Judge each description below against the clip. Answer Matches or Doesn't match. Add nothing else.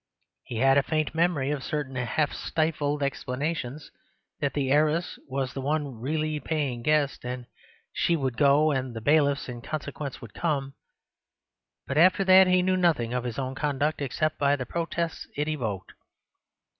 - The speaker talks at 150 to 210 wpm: Matches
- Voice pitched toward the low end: Doesn't match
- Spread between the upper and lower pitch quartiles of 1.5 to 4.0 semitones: Matches